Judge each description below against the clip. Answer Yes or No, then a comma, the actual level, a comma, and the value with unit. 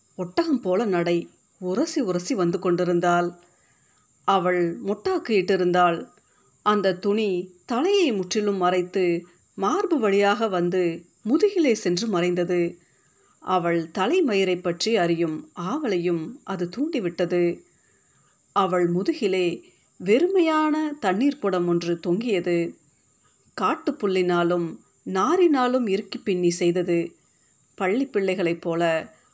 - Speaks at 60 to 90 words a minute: Yes, average, 85 wpm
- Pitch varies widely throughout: No, average, 4.3 semitones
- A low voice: No, medium, 185 Hz